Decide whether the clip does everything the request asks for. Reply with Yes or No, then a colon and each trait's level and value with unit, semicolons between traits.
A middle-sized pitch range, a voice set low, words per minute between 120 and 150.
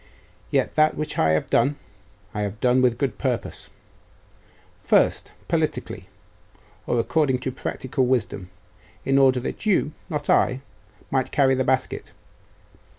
No: narrow, 2.1 semitones; low, 130 Hz; average, 140 wpm